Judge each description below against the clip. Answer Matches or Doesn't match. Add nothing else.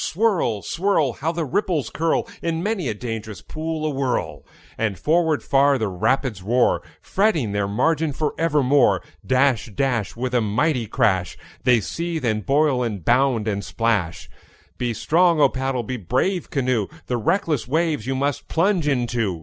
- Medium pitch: Doesn't match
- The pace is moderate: Matches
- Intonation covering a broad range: Matches